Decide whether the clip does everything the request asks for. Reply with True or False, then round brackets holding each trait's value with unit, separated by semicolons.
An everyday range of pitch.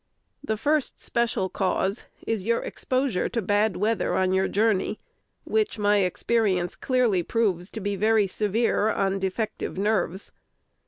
True (3.1 semitones)